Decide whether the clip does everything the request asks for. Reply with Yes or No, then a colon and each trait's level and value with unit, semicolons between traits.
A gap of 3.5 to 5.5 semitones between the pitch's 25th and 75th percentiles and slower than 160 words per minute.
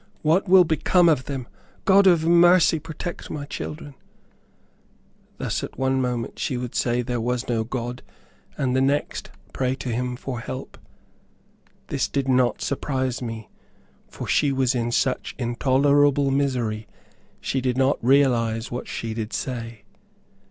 No: average, 2.9 semitones; average, 145 wpm